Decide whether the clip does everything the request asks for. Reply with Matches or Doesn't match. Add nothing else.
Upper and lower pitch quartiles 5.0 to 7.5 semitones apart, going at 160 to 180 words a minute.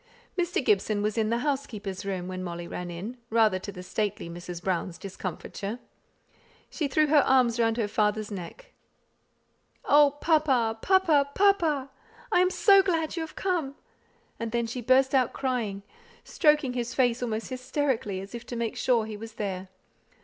Matches